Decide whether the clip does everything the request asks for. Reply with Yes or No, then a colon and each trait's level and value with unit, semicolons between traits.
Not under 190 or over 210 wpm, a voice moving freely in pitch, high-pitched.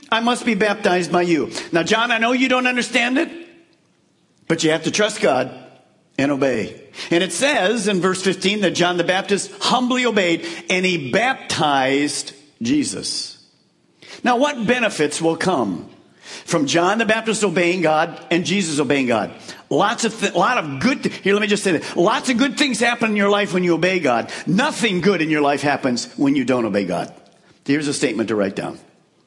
Yes: average, 195 wpm; wide, 6.1 semitones; high, 195 Hz